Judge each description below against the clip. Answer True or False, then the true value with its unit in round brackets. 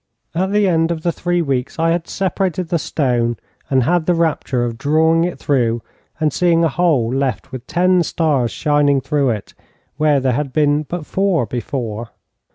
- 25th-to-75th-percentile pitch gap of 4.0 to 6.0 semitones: True (4.6 semitones)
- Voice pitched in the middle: True (150 Hz)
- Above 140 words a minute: True (175 wpm)